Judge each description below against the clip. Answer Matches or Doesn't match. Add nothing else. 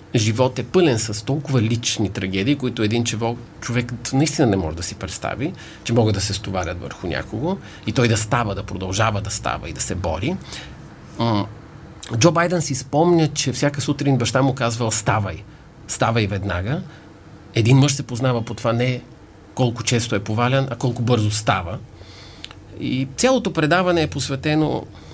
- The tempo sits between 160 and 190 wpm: Matches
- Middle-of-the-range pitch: Doesn't match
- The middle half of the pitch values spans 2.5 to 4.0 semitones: Doesn't match